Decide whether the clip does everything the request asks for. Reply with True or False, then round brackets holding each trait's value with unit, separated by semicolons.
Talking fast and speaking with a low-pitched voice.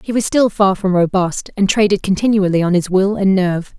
False (220 wpm; 195 Hz)